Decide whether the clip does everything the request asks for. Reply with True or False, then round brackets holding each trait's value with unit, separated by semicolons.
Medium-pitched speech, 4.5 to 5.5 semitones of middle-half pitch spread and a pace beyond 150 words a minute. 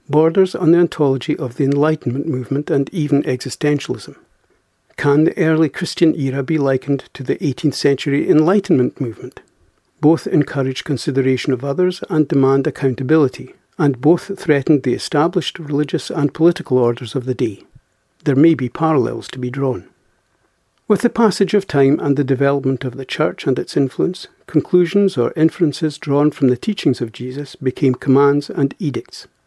False (145 Hz; 3.2 semitones; 160 wpm)